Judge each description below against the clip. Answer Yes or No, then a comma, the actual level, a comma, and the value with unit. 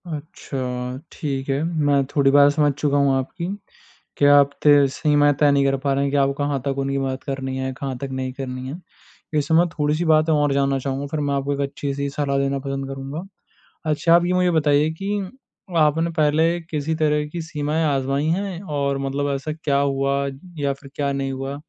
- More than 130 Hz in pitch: Yes, medium, 140 Hz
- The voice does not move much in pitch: Yes, narrow, 1.7 semitones